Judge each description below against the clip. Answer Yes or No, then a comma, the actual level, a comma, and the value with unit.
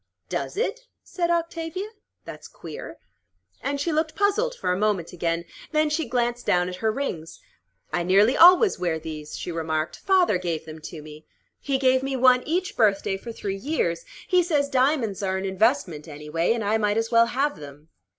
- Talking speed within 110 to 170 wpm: No, average, 185 wpm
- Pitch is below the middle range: No, high, 225 Hz